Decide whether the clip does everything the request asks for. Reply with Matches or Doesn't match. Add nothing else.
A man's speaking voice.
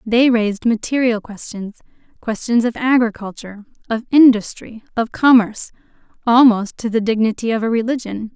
Doesn't match